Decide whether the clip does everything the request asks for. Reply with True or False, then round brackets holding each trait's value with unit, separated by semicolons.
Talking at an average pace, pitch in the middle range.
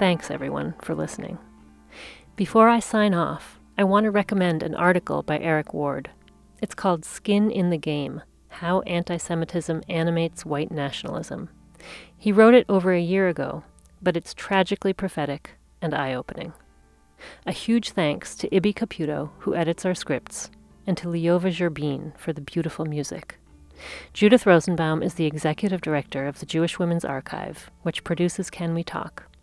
True (155 wpm; 170 Hz)